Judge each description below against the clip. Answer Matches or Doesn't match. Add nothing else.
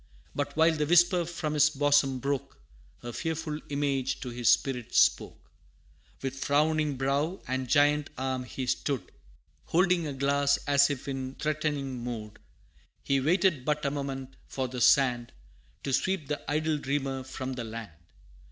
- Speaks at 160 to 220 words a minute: Doesn't match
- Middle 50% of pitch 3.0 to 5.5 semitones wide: Doesn't match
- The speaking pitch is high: Doesn't match